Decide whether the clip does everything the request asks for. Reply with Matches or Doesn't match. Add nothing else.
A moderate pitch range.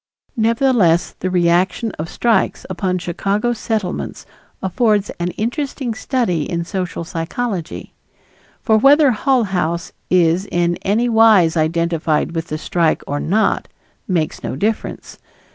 Matches